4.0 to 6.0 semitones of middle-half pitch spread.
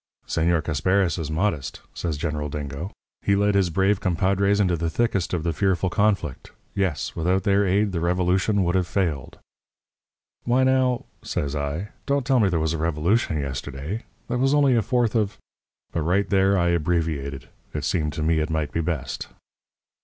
Yes: average, 4.4 semitones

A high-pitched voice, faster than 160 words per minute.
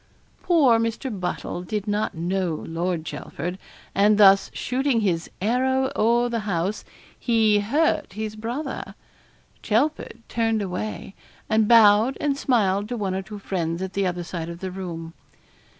No: high, 210 Hz; average, 150 wpm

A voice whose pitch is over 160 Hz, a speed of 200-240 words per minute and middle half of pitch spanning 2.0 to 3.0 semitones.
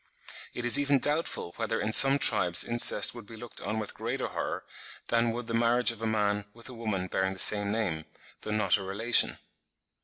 No: low, 115 Hz; fast, 205 wpm; average, 2.7 semitones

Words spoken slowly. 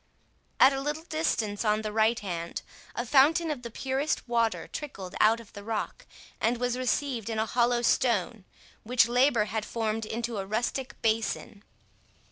No: average, 165 wpm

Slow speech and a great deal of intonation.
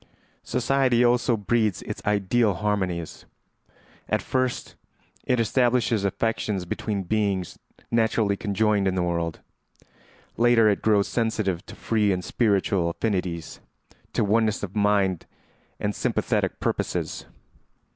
No: slow, 115 wpm; average, 3.2 semitones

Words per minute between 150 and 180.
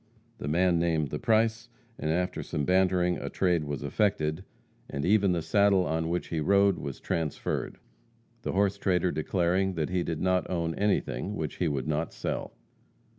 Yes: average, 175 wpm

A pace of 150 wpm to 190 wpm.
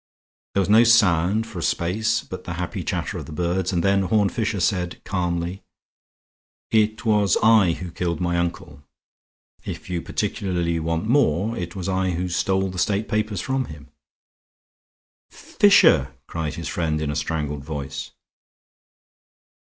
Yes: average, 155 wpm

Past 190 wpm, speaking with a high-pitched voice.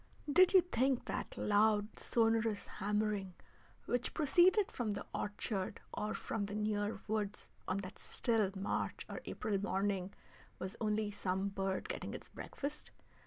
No: average, 140 wpm; high, 210 Hz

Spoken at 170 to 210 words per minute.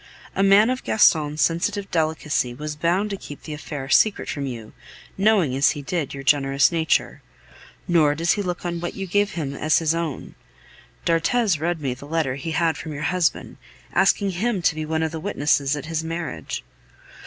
Yes: average, 190 wpm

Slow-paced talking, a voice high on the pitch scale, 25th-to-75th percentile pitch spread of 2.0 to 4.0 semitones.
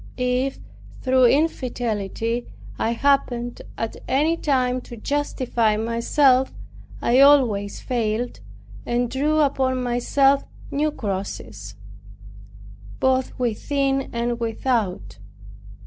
Yes: slow, 90 wpm; very high, 250 Hz; average, 2.9 semitones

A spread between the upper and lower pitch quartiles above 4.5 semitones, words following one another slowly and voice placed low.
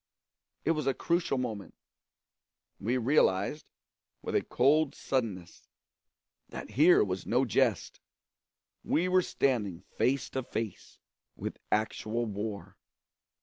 Yes: wide, 5.4 semitones; slow, 110 wpm; low, 125 Hz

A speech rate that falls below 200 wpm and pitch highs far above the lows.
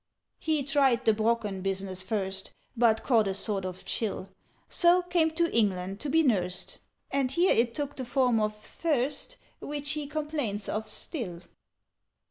Yes: average, 155 wpm; wide, 6.4 semitones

